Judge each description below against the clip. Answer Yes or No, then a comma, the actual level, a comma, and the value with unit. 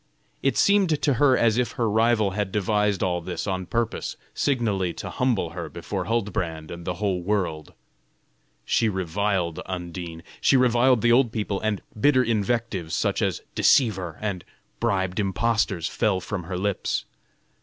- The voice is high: No, low, 105 Hz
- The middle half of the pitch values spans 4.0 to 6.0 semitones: Yes, average, 4.5 semitones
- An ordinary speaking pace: Yes, average, 155 wpm